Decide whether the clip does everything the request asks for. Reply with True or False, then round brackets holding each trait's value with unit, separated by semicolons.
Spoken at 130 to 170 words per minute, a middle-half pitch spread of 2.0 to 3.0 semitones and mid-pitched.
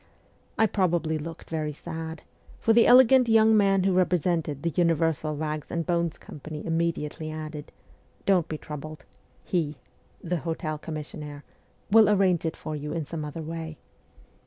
True (155 wpm; 2.7 semitones; 165 Hz)